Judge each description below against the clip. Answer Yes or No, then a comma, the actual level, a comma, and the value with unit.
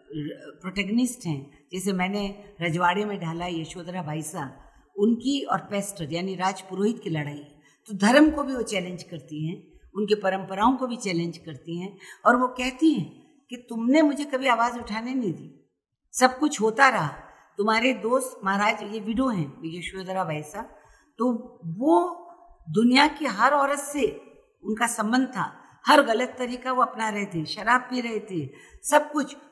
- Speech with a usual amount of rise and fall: No, wide, 6.0 semitones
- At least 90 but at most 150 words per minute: No, average, 160 wpm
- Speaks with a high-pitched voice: Yes, high, 215 Hz